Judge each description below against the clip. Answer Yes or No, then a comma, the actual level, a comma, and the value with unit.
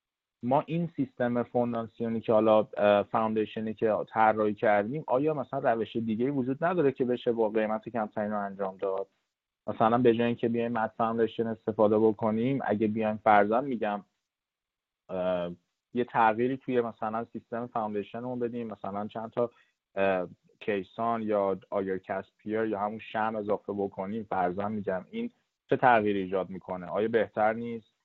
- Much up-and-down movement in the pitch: No, narrow, 2.4 semitones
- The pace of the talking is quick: No, average, 145 wpm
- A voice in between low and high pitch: No, low, 110 Hz